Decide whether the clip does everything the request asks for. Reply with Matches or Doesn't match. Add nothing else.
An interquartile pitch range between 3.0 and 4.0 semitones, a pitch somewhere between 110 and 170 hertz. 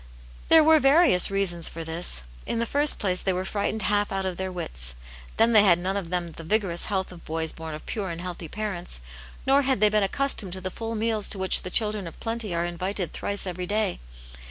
Doesn't match